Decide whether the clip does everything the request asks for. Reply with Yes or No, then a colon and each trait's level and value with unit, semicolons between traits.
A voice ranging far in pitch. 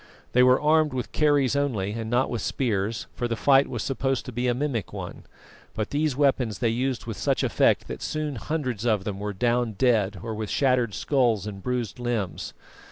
No: average, 3.7 semitones